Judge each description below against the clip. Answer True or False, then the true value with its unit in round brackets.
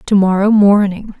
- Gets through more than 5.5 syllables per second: False (4.6 syllables/s)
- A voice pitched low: False (200 Hz)